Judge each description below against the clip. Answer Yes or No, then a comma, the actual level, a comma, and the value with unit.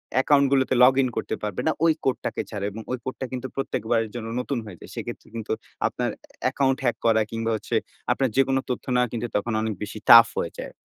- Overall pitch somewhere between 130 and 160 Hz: No, low, 120 Hz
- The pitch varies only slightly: No, average, 3.0 semitones